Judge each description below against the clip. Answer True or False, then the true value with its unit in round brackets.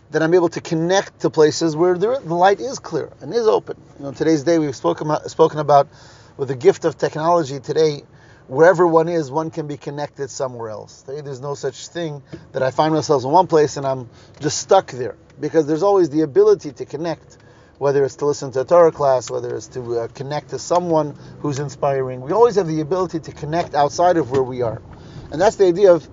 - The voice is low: False (155 Hz)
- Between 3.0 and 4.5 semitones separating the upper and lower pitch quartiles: True (3.4 semitones)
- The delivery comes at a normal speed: False (225 wpm)